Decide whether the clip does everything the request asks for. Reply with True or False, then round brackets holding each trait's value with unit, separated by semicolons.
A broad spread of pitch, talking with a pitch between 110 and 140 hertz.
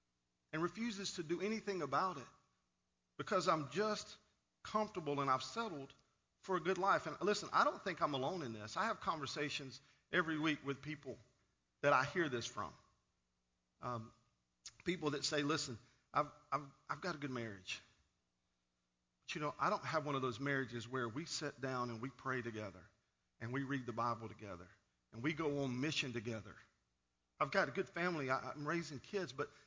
True (6.5 semitones; 135 Hz)